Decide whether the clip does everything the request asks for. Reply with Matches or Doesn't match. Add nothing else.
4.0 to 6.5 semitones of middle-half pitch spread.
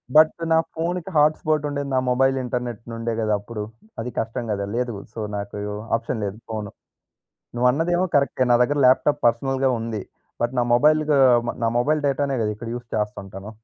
Matches